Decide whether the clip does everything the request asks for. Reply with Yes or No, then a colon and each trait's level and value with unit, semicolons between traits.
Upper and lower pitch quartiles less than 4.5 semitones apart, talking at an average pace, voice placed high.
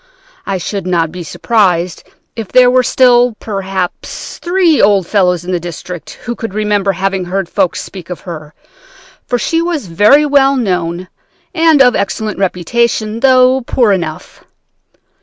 No: wide, 5.6 semitones; average, 150 wpm; high, 200 Hz